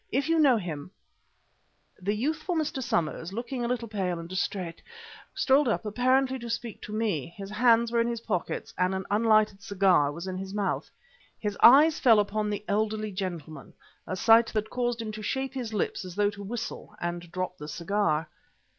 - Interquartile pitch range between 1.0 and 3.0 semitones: No, average, 4.2 semitones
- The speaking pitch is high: Yes, high, 210 Hz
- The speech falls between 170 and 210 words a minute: Yes, average, 190 wpm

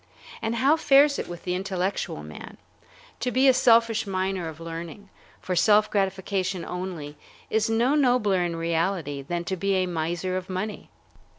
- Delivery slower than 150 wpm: No, average, 165 wpm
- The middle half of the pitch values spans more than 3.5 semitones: Yes, average, 4.2 semitones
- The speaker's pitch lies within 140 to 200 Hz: Yes, high, 190 Hz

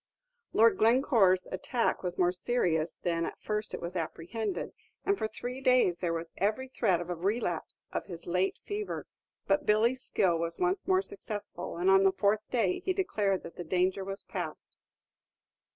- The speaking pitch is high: Yes, high, 195 Hz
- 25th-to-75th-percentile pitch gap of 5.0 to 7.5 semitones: Yes, wide, 5.4 semitones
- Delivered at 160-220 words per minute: Yes, average, 175 wpm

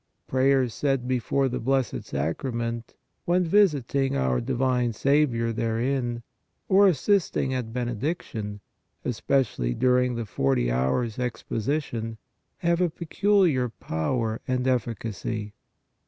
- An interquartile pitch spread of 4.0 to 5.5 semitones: No, average, 3.4 semitones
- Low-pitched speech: Yes, low, 125 Hz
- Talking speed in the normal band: No, slow, 105 wpm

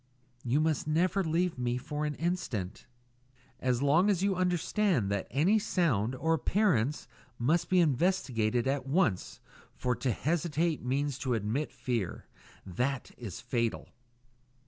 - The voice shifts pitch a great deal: Yes, wide, 6.1 semitones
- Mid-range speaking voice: Yes, medium, 145 Hz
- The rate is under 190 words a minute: Yes, average, 140 wpm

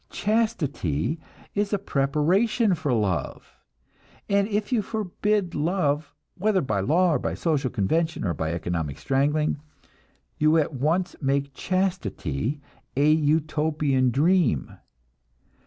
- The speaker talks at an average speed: No, slow, 115 wpm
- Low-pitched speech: No, medium, 155 Hz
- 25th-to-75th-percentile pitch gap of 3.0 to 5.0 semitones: No, wide, 5.6 semitones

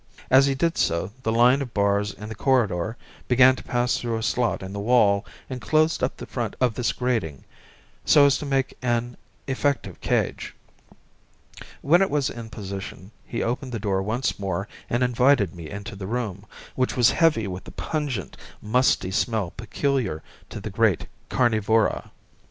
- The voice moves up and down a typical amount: Yes, average, 4.2 semitones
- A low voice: Yes, low, 120 Hz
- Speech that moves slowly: No, average, 175 wpm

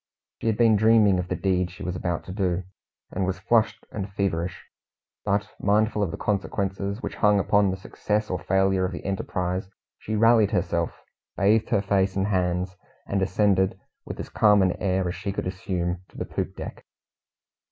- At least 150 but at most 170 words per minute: No, average, 185 wpm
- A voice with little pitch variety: Yes, narrow, 2.0 semitones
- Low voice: Yes, very low, 95 Hz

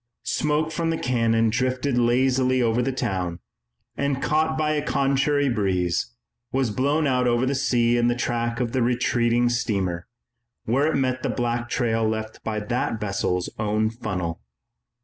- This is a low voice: Yes, low, 120 Hz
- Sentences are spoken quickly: No, average, 160 wpm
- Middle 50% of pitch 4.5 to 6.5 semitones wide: No, average, 3.2 semitones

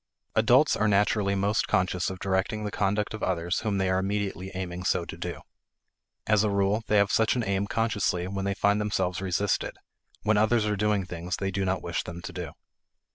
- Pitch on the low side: Yes, low, 100 Hz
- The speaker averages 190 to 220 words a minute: Yes, fast, 205 wpm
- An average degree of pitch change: No, narrow, 2.1 semitones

